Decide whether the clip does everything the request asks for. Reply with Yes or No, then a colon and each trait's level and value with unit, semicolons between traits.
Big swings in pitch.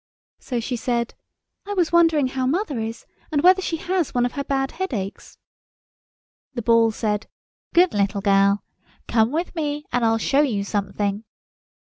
Yes: wide, 6.0 semitones